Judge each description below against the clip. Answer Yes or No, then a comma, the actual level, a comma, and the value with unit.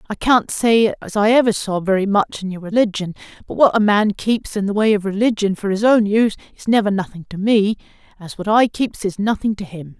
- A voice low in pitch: No, high, 205 Hz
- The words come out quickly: Yes, fast, 230 wpm